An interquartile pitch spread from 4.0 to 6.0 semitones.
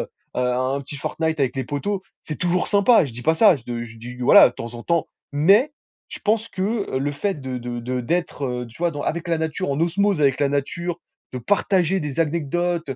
Yes: wide, 5.6 semitones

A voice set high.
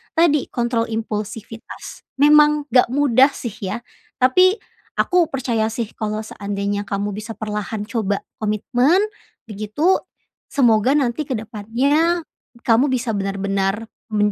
Yes: high, 225 Hz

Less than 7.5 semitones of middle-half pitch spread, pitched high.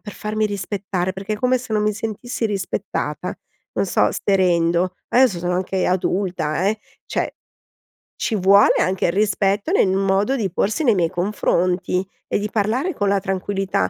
Yes: narrow, 2.5 semitones; high, 195 Hz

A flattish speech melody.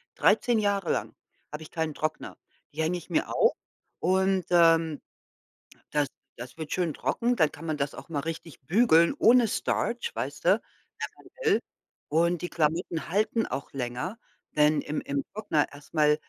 No: average, 4.0 semitones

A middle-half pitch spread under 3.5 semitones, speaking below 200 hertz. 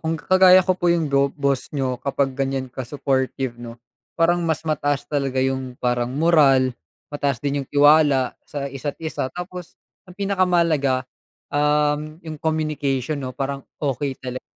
Yes: average, 3.1 semitones; medium, 140 Hz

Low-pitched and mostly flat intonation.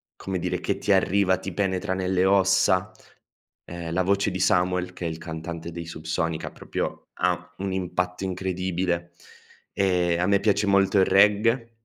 Yes: very low, 95 Hz; narrow, 2.0 semitones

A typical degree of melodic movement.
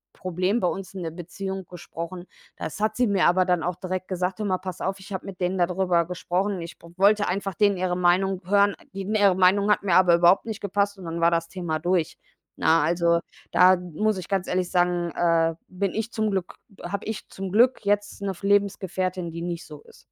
No: narrow, 2.3 semitones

